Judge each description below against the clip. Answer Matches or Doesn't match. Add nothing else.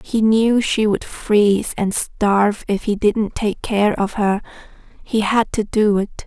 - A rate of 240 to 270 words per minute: Doesn't match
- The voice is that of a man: Doesn't match